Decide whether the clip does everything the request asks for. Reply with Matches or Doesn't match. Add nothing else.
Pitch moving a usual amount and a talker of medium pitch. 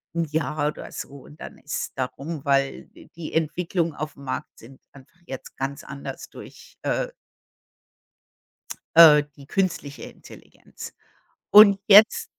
Matches